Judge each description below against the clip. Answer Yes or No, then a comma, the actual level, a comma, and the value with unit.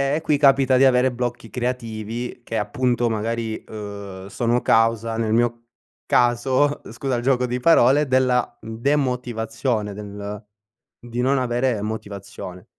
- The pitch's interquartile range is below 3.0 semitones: Yes, narrow, 2.5 semitones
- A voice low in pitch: Yes, low, 120 Hz